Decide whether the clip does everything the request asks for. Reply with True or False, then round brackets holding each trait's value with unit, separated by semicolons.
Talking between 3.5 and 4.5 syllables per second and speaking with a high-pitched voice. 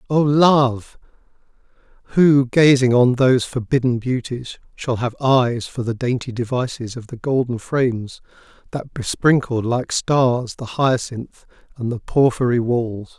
False (4.1 syllables/s; 125 Hz)